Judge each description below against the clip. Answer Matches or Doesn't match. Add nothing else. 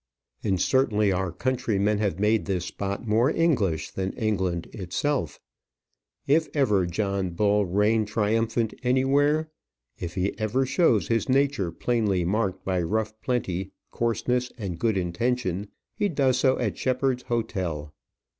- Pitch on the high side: Doesn't match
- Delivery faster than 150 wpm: Doesn't match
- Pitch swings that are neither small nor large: Matches